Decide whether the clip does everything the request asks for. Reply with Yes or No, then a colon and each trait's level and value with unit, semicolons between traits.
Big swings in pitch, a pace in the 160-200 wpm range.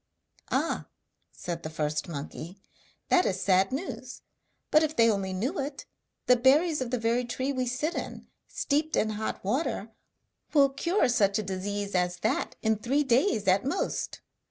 Yes: wide, 6.0 semitones; average, 165 wpm